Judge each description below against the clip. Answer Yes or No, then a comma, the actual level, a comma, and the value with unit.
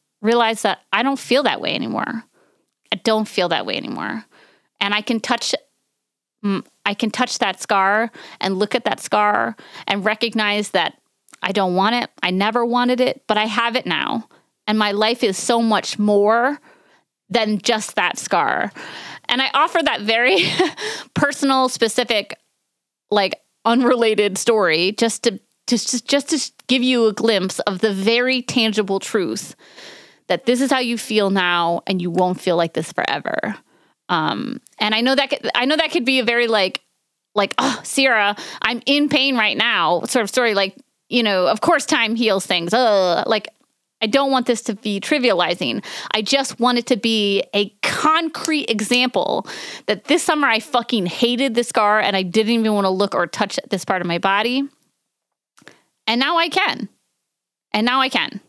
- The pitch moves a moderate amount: Yes, average, 3.7 semitones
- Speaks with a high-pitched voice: Yes, high, 230 Hz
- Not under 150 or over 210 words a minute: Yes, average, 175 wpm